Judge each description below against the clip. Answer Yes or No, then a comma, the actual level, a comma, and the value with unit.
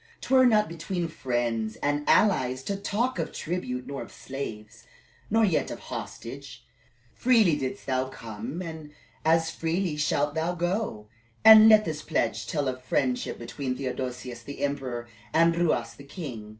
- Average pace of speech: Yes, average, 155 wpm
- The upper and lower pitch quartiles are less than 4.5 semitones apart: No, wide, 5.5 semitones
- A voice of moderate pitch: Yes, medium, 150 Hz